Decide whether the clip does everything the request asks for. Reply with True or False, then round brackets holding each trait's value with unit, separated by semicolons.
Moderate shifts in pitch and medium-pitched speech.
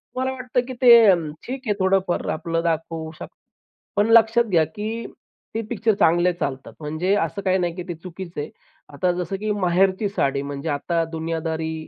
True (4.3 semitones; 180 Hz)